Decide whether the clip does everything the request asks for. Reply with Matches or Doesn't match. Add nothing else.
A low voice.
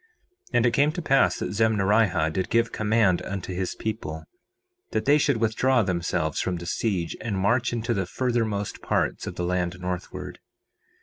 Matches